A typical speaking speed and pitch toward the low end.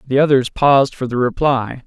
Yes: average, 195 wpm; low, 130 Hz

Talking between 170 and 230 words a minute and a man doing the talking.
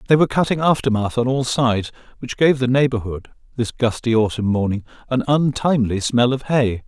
Yes: average, 175 wpm; male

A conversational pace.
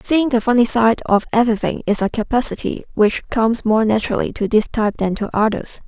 Yes: average, 195 wpm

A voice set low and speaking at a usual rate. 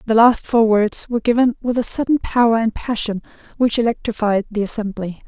No: high, 225 Hz; average, 180 wpm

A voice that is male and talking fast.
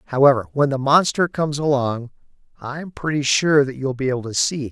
Yes: male; fast, 230 wpm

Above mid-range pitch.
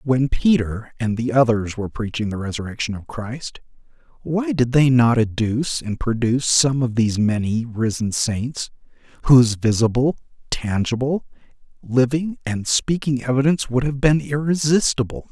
No: low, 125 Hz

